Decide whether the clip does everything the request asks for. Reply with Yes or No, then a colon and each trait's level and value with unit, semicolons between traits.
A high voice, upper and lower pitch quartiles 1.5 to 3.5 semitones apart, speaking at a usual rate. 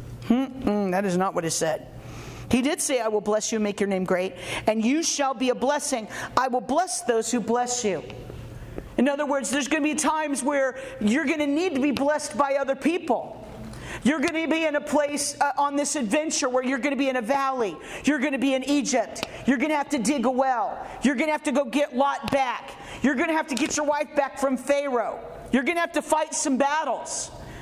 No: very high, 275 Hz; average, 3.2 semitones; fast, 245 wpm